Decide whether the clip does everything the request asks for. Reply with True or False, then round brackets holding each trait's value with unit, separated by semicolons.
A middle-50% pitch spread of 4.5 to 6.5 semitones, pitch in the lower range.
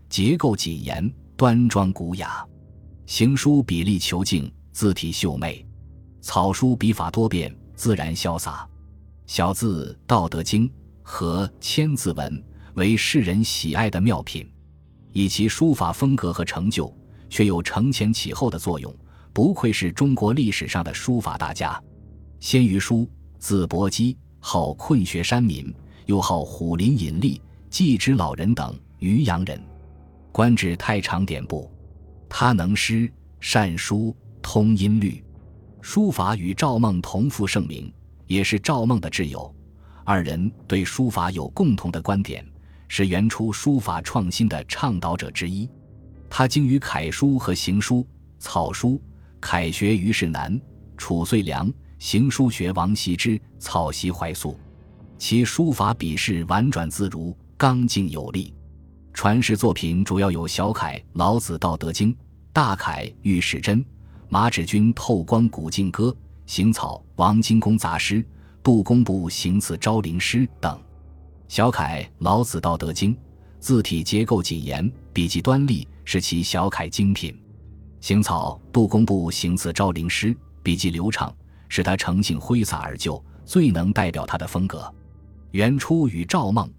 True (5.2 semitones; 95 Hz)